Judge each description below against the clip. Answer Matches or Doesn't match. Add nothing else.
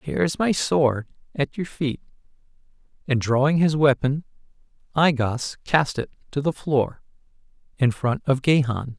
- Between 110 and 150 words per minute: Matches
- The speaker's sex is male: Matches